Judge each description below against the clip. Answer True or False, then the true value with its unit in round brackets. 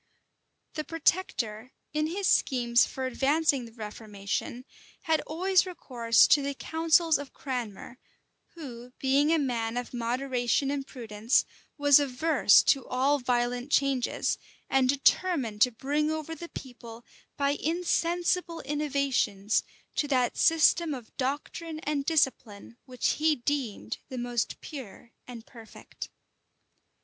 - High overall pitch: True (270 Hz)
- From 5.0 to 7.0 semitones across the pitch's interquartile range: False (4.1 semitones)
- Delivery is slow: True (125 wpm)